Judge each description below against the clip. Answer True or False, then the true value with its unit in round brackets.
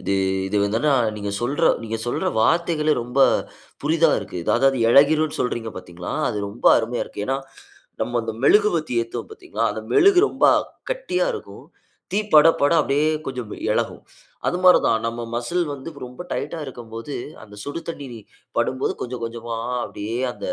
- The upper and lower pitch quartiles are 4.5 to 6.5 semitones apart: True (5.1 semitones)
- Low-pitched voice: True (125 Hz)